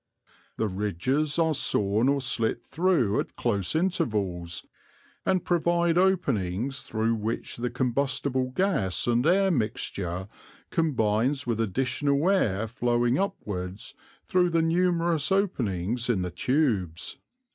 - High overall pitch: No, low, 125 Hz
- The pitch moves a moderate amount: No, wide, 7.7 semitones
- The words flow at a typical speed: No, slow, 115 wpm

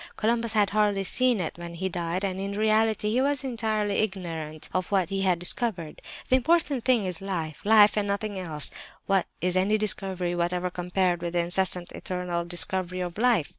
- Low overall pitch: No, high, 190 Hz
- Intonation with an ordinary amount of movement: Yes, average, 3.4 semitones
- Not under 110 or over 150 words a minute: No, average, 180 wpm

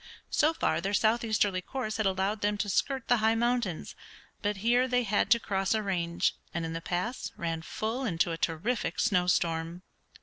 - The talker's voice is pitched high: Yes, high, 205 Hz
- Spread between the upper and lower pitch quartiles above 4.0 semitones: Yes, average, 4.7 semitones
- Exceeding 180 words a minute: Yes, average, 190 wpm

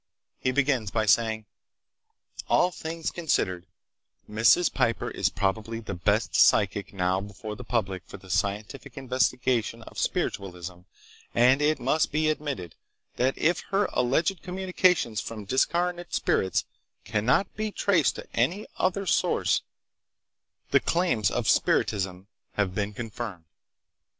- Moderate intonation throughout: No, wide, 7.3 semitones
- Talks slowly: Yes, slow, 125 wpm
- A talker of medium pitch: No, low, 115 Hz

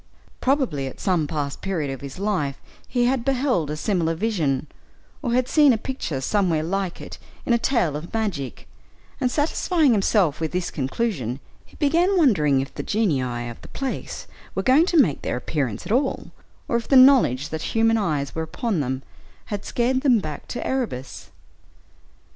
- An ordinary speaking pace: Yes, average, 175 wpm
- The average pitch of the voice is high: Yes, high, 195 Hz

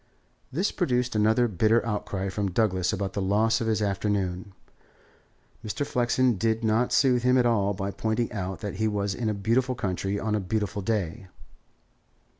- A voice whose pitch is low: Yes, low, 105 Hz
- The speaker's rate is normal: Yes, average, 170 wpm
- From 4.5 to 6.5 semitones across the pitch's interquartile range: No, average, 3.1 semitones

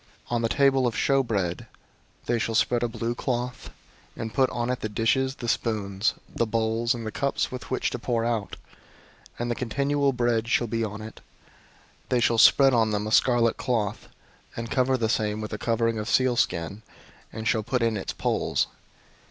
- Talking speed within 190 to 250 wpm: Yes, average, 195 wpm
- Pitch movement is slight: Yes, narrow, 2.1 semitones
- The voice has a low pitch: Yes, low, 115 Hz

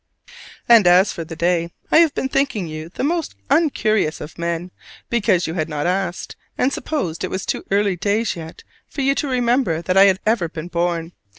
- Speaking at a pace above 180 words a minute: Yes, average, 200 wpm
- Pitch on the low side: No, medium, 185 Hz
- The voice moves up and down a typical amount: No, wide, 5.8 semitones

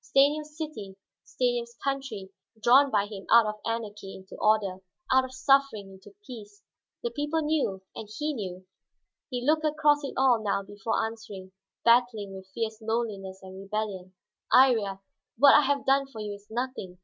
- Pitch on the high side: Yes, high, 225 Hz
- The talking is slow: No, average, 165 wpm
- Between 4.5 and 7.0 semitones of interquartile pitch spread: Yes, average, 5.3 semitones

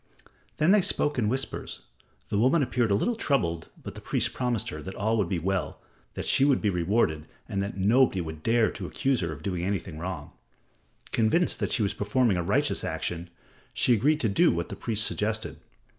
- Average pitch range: No, wide, 5.8 semitones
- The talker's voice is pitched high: No, low, 105 Hz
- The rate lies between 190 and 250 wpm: Yes, fast, 205 wpm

